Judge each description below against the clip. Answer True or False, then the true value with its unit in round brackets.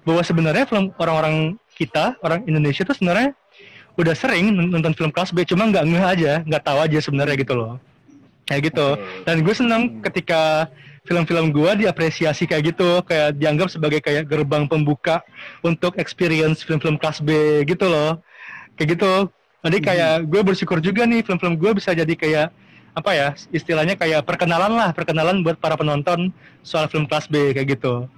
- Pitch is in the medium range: True (165 Hz)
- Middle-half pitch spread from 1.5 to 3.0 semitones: True (2.7 semitones)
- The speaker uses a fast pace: True (165 wpm)